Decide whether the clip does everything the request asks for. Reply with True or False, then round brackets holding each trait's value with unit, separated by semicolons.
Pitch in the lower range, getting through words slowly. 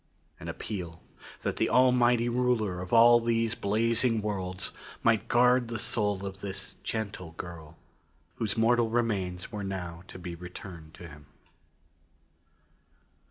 True (105 Hz; 130 wpm)